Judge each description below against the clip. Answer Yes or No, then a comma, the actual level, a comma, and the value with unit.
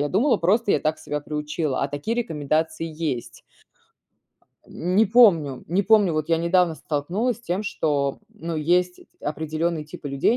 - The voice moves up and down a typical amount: Yes, average, 3.8 semitones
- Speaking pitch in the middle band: Yes, medium, 165 Hz